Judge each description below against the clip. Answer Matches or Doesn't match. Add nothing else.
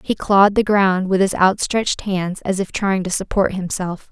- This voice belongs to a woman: Matches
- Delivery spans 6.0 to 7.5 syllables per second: Doesn't match